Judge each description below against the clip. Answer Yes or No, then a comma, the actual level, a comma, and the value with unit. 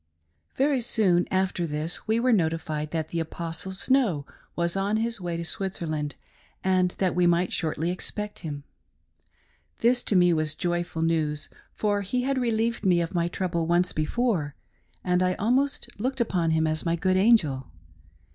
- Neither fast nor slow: Yes, average, 165 wpm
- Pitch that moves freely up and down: No, average, 4.5 semitones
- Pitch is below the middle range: No, medium, 180 Hz